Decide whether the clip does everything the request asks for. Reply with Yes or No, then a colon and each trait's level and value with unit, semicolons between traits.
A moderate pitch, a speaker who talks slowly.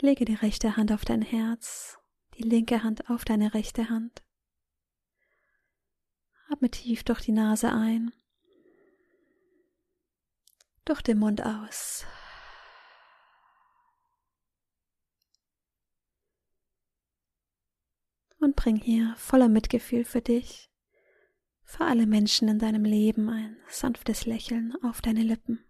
No: high, 235 Hz; slow, 100 wpm